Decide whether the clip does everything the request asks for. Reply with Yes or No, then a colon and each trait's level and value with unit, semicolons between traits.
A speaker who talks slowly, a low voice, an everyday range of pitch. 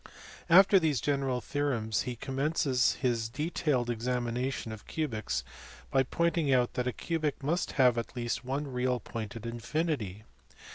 No: average, 145 wpm; low, 125 Hz; average, 3.8 semitones